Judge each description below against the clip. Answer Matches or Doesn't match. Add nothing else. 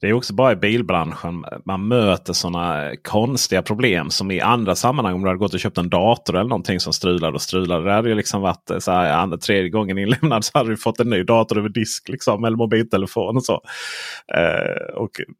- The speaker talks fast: Matches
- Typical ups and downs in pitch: Matches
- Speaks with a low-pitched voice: Matches